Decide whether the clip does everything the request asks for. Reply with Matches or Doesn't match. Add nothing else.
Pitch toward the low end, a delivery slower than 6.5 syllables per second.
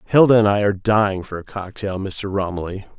Matches